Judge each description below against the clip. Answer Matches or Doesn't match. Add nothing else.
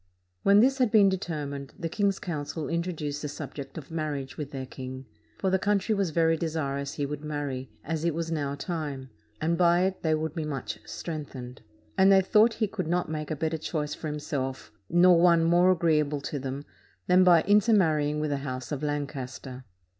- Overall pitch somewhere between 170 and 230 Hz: Doesn't match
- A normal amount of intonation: Matches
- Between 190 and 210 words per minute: Matches